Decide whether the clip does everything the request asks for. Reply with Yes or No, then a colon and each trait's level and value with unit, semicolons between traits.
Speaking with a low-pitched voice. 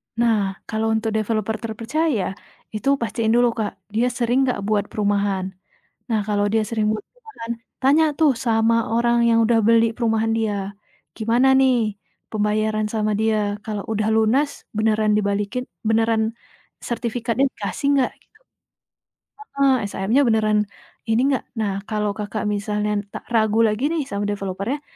No: high, 220 Hz